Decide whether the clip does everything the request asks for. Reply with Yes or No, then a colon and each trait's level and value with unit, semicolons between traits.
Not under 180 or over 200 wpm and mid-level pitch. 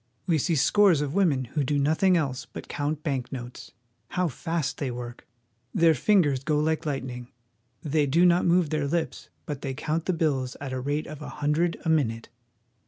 Yes: average, 195 wpm; medium, 150 Hz